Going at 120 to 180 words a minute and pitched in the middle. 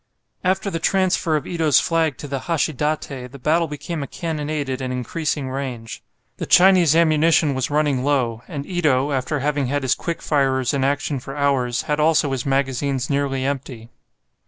Yes: average, 175 wpm; medium, 145 Hz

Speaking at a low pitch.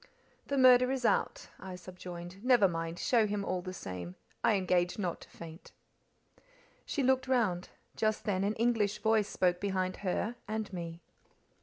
No: high, 195 Hz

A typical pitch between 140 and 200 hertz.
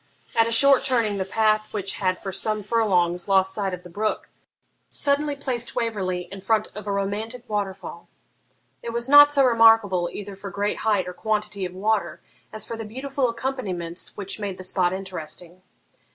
No: high, 210 Hz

